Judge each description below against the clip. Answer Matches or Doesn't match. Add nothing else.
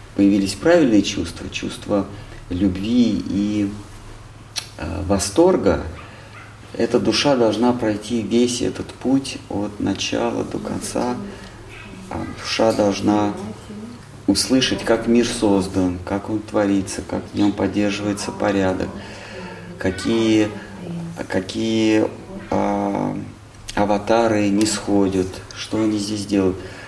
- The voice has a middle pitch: Doesn't match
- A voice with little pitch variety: Matches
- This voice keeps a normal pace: Doesn't match